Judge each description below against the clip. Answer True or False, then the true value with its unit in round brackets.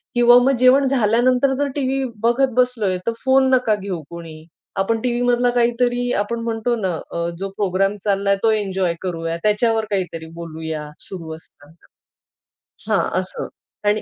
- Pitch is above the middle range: True (215 Hz)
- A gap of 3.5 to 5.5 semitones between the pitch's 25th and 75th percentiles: True (5.0 semitones)